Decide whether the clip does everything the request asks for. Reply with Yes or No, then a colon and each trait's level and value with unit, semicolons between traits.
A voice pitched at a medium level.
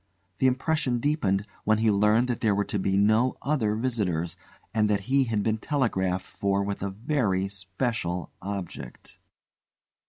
No: low, 105 Hz